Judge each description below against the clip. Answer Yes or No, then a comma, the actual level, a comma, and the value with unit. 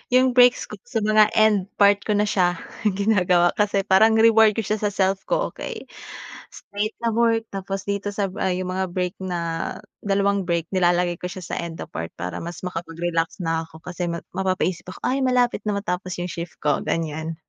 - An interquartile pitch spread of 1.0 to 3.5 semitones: Yes, average, 3.2 semitones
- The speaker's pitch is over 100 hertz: Yes, high, 190 Hz